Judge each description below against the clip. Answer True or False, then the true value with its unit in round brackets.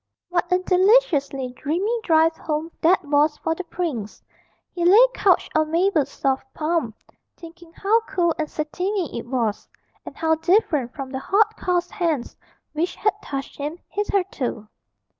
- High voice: True (330 Hz)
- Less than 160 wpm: True (150 wpm)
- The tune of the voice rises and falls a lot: False (4.2 semitones)